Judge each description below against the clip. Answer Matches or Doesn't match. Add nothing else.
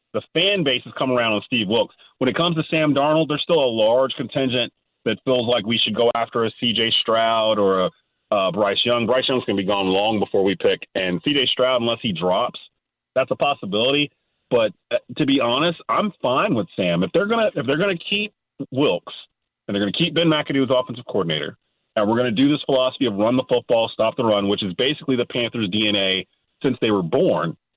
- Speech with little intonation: Doesn't match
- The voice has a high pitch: Doesn't match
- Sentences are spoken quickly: Matches